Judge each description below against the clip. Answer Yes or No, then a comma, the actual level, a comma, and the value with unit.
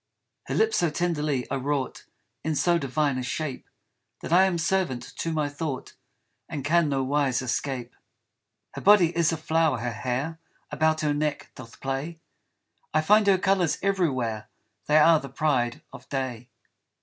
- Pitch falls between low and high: Yes, medium, 150 Hz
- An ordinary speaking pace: Yes, average, 160 wpm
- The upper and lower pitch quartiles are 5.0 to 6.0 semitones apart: No, average, 4.1 semitones